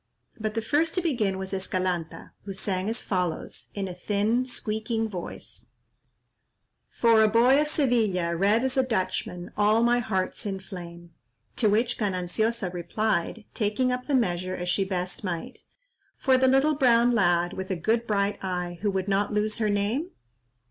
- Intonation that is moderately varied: Yes, average, 4.0 semitones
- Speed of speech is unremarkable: Yes, average, 170 wpm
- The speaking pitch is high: Yes, high, 210 Hz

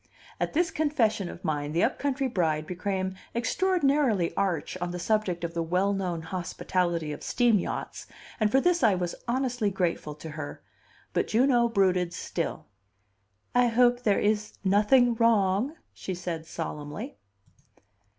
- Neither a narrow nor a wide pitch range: No, wide, 5.8 semitones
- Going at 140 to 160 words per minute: Yes, average, 150 wpm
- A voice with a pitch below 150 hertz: No, high, 195 Hz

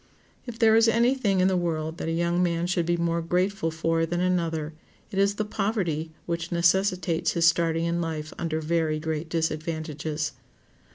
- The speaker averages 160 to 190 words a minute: Yes, average, 180 wpm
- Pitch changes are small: Yes, narrow, 2.2 semitones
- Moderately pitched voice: Yes, medium, 170 Hz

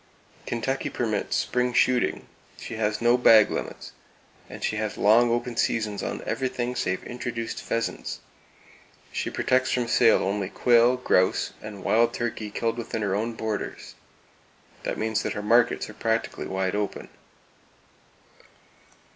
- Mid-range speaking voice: No, low, 115 Hz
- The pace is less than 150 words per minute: Yes, average, 140 wpm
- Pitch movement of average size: No, narrow, 2.2 semitones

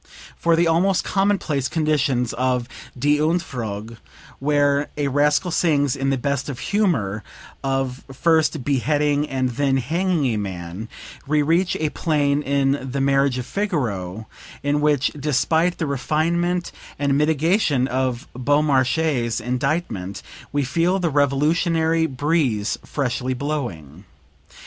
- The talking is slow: Yes, slow, 125 wpm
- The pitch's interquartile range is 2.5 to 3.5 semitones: No, average, 3.9 semitones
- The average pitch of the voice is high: No, medium, 140 Hz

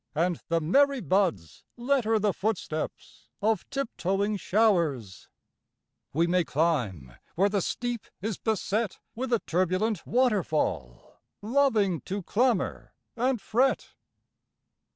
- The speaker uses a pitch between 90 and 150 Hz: No, high, 200 Hz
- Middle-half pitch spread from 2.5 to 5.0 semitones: No, wide, 5.4 semitones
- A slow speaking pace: Yes, slow, 115 wpm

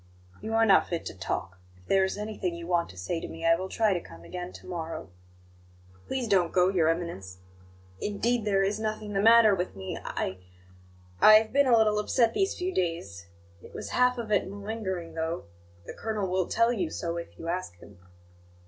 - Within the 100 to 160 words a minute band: No, fast, 205 wpm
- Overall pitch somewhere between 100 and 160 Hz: No, high, 190 Hz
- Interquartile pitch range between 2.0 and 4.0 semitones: No, average, 4.6 semitones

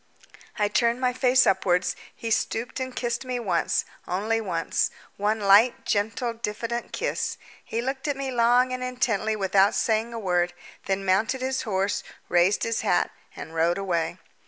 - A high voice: Yes, high, 225 Hz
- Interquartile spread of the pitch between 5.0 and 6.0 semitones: No, average, 4.1 semitones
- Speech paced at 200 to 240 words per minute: No, average, 160 wpm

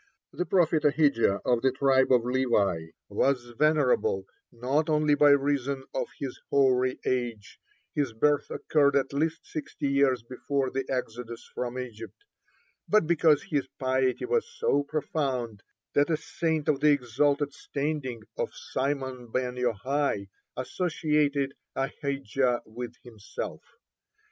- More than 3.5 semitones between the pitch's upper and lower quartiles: No, average, 2.8 semitones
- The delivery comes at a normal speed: No, slow, 130 wpm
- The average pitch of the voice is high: No, low, 135 Hz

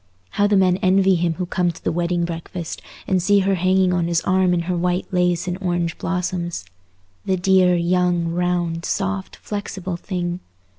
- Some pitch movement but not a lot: No, narrow, 1.4 semitones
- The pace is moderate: Yes, average, 180 wpm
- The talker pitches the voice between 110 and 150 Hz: No, medium, 180 Hz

